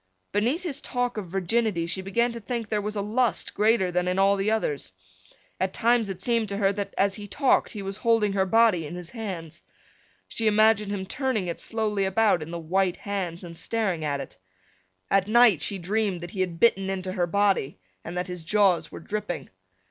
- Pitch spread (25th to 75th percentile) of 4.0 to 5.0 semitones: No, average, 3.5 semitones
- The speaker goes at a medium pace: No, fast, 210 wpm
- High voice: Yes, high, 200 Hz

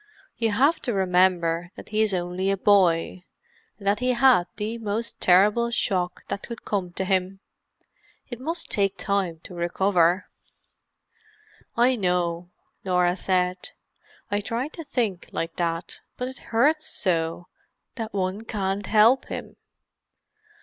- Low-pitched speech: No, high, 195 Hz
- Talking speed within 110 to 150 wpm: Yes, slow, 135 wpm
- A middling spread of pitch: Yes, average, 4.1 semitones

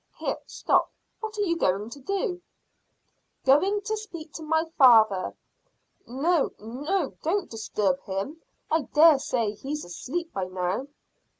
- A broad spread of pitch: Yes, wide, 7.9 semitones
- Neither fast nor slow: No, slow, 130 wpm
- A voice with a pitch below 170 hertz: No, very high, 295 Hz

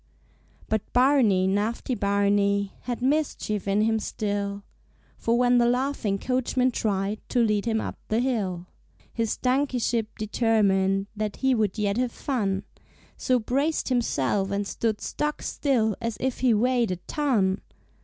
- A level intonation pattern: No, average, 3.7 semitones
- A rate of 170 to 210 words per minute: No, average, 145 wpm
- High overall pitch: Yes, high, 220 Hz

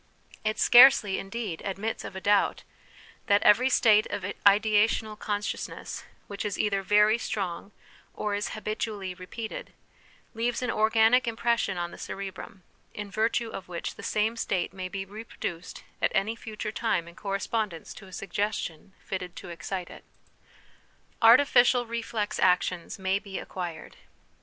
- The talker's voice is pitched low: No, high, 205 Hz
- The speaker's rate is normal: Yes, average, 145 wpm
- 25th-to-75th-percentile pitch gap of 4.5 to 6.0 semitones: No, average, 2.7 semitones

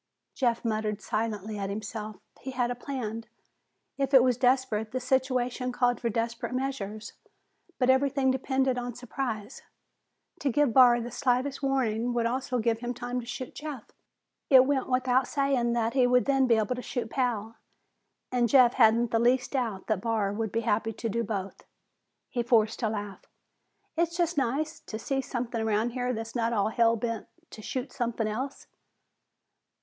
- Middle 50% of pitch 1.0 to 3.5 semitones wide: Yes, narrow, 2.6 semitones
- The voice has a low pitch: No, high, 240 Hz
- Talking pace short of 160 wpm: No, average, 170 wpm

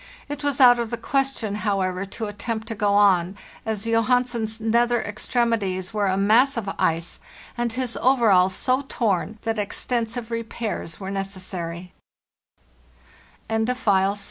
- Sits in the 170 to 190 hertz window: No, high, 225 Hz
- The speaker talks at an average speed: No, slow, 125 wpm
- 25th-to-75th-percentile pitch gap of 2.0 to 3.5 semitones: Yes, average, 3.1 semitones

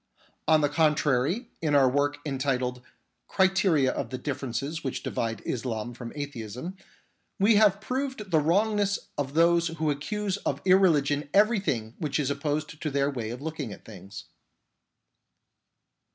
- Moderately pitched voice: Yes, medium, 150 Hz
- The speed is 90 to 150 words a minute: Yes, average, 140 wpm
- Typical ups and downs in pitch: No, wide, 5.9 semitones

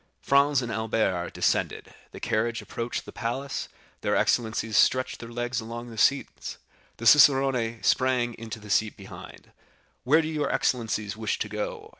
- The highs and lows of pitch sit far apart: No, average, 2.8 semitones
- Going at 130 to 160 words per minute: Yes, average, 155 wpm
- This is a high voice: No, low, 115 Hz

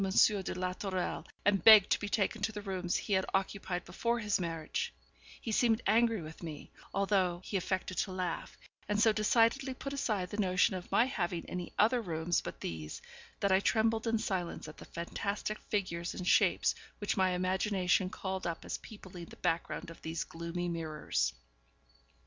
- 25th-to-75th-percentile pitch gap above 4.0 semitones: No, average, 3.3 semitones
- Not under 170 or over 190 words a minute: Yes, average, 180 wpm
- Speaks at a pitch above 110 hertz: Yes, high, 190 Hz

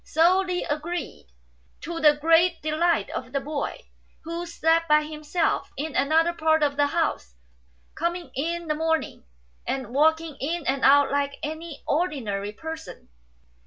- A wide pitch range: No, average, 2.7 semitones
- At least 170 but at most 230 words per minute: No, average, 145 wpm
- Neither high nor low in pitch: No, very high, 315 Hz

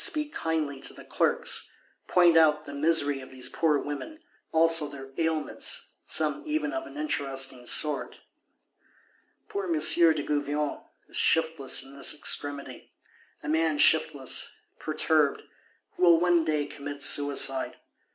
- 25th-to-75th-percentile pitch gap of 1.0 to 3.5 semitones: Yes, narrow, 2.5 semitones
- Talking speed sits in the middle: No, slow, 130 wpm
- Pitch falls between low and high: Yes, medium, 150 Hz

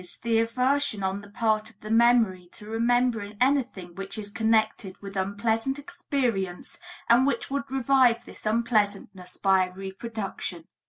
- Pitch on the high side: Yes, high, 220 Hz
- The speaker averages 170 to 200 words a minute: No, average, 145 wpm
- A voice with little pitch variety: No, average, 3.7 semitones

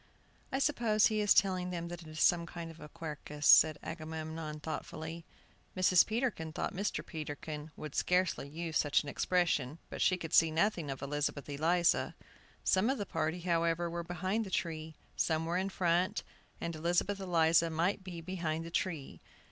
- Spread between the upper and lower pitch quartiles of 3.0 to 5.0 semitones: No, narrow, 2.6 semitones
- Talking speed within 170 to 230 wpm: Yes, average, 175 wpm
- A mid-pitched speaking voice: Yes, medium, 170 Hz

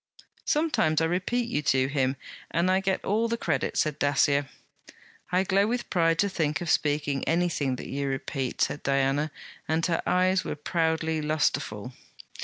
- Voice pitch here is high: No, medium, 160 Hz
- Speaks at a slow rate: No, average, 165 wpm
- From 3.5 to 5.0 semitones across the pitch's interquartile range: Yes, average, 4.4 semitones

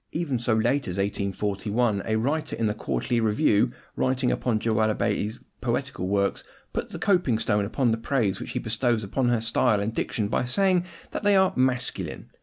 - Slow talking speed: No, average, 185 wpm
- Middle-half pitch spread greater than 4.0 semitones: No, average, 3.6 semitones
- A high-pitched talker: No, low, 115 Hz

